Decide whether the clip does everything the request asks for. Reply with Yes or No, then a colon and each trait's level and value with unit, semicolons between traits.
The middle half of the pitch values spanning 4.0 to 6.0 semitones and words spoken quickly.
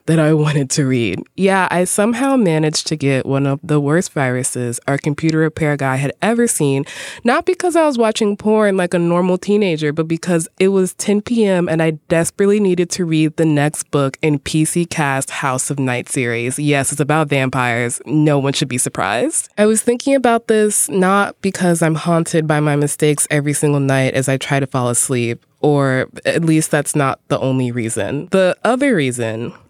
No: average, 5.2 semitones; average, 195 wpm